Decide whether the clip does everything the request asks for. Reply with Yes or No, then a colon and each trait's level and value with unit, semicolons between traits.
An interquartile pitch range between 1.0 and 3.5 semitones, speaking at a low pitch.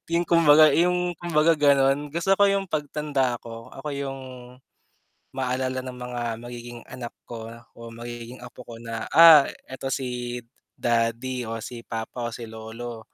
No: average, 3.9 semitones; low, 125 Hz